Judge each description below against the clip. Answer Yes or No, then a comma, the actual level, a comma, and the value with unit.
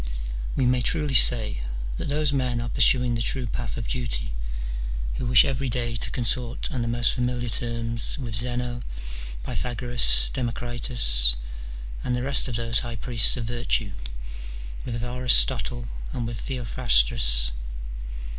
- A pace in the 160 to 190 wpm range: No, average, 140 wpm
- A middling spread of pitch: No, narrow, 1.7 semitones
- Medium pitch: No, low, 120 Hz